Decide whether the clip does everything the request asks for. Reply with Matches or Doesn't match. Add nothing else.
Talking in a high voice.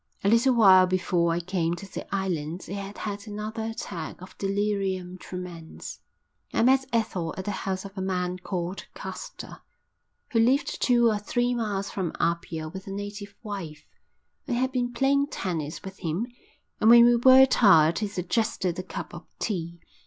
Matches